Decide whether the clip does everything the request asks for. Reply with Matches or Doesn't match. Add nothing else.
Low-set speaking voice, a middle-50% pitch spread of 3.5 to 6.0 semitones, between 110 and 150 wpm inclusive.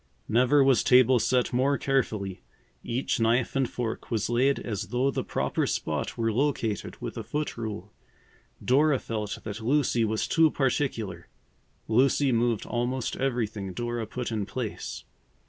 Doesn't match